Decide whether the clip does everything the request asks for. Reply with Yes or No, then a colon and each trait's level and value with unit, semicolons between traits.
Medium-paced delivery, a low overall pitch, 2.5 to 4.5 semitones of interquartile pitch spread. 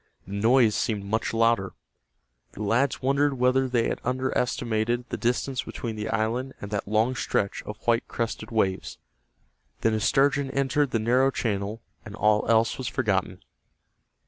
Yes: average, 155 wpm; low, 115 Hz; average, 3.3 semitones